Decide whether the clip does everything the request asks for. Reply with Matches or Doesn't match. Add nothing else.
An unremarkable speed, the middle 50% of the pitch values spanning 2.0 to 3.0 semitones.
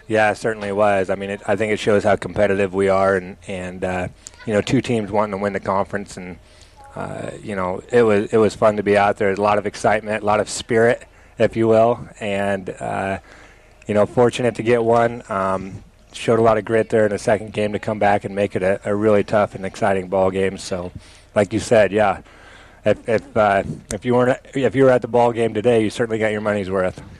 Doesn't match